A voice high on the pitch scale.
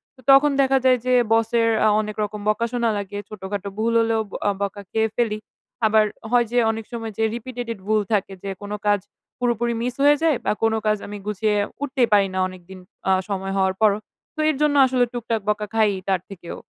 Yes: high, 220 Hz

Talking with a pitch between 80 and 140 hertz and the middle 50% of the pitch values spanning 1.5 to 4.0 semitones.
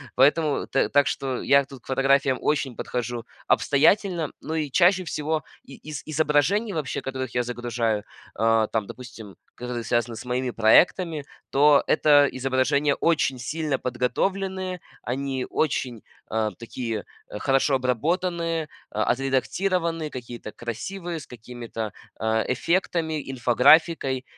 No: low, 135 Hz; average, 4.5 semitones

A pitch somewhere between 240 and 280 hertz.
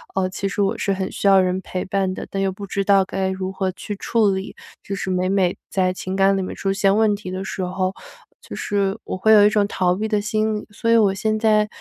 No: high, 195 Hz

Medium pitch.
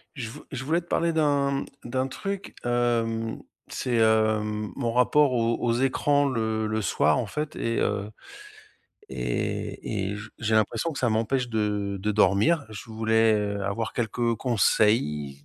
No: low, 115 Hz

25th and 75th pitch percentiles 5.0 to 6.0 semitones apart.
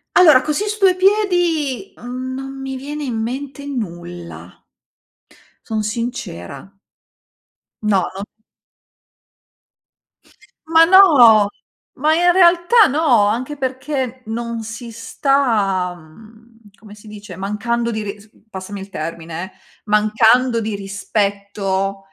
Yes: wide, 5.5 semitones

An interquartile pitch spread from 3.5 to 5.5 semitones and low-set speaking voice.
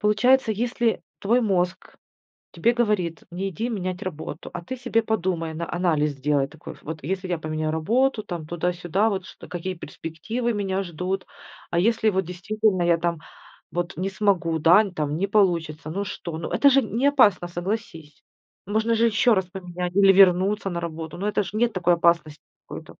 No: average, 4.0 semitones; medium, 185 Hz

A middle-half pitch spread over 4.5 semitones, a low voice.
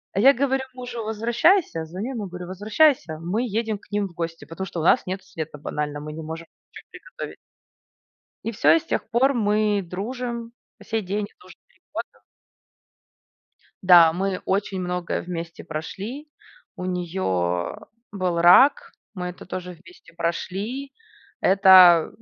No: average, 5.0 semitones; high, 190 Hz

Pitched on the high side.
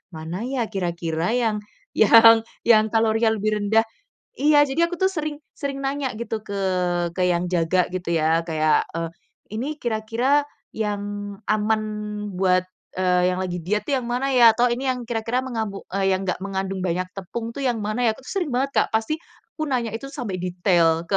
Yes: high, 215 Hz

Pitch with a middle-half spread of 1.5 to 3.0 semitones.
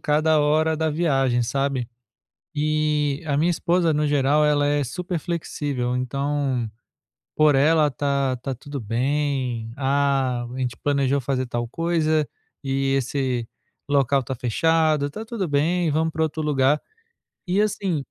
Yes: average, 2.7 semitones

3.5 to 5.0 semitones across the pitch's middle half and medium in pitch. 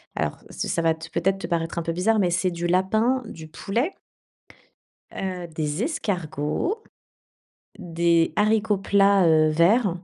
Yes: average, 4.0 semitones; medium, 180 Hz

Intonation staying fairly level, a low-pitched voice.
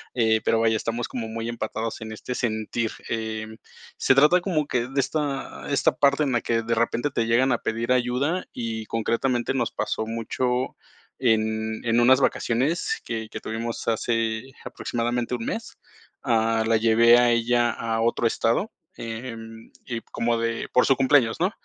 Yes: narrow, 2.1 semitones; low, 115 Hz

